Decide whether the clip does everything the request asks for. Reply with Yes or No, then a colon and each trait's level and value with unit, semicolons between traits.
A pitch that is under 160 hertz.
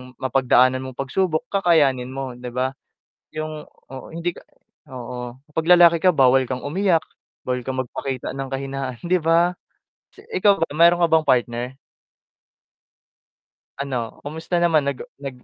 Yes: medium, 140 Hz